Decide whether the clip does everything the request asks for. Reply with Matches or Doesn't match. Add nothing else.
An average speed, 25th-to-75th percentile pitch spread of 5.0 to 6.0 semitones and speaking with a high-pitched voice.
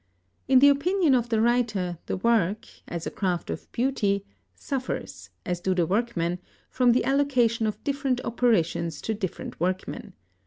Matches